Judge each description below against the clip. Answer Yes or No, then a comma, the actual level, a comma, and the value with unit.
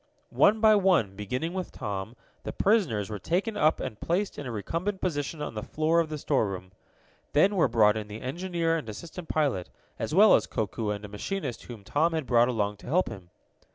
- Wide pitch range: Yes, wide, 8.5 semitones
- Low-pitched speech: No, medium, 145 Hz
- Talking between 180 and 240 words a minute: Yes, fast, 205 wpm